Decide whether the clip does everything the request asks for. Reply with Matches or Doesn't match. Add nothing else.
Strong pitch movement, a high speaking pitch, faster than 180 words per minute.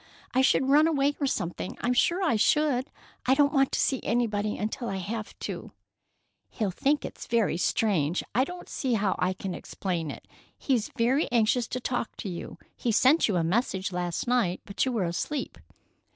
Matches